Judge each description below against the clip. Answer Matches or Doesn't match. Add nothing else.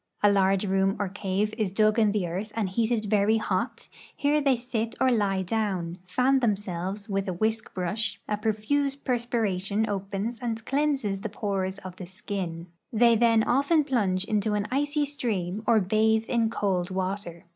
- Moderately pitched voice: Doesn't match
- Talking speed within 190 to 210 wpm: Doesn't match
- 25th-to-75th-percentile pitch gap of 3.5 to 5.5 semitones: Doesn't match